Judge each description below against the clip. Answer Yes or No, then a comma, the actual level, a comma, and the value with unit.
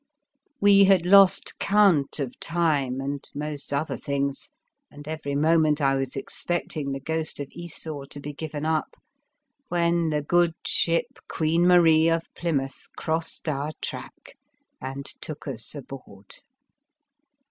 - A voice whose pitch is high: No, medium, 155 Hz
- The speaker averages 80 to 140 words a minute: Yes, slow, 135 wpm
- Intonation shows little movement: No, average, 3.1 semitones